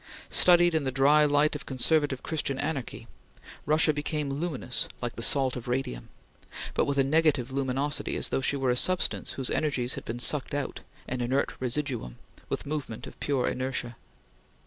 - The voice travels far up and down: No, average, 2.8 semitones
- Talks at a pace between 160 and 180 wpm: Yes, average, 170 wpm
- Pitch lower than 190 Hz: Yes, low, 135 Hz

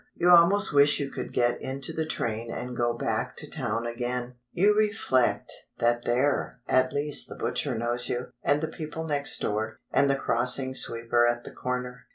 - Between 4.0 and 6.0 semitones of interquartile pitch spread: No, average, 3.4 semitones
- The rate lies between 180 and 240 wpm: Yes, average, 185 wpm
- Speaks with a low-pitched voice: Yes, low, 125 Hz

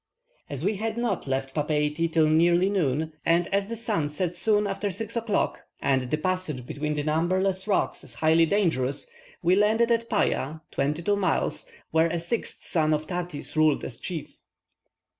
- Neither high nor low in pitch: Yes, medium, 170 Hz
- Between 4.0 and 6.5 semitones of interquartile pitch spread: Yes, average, 4.7 semitones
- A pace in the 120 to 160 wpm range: No, average, 170 wpm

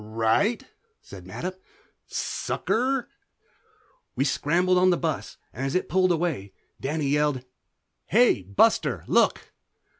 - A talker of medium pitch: Yes, medium, 160 Hz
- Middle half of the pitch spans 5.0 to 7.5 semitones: Yes, wide, 5.4 semitones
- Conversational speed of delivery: No, slow, 115 wpm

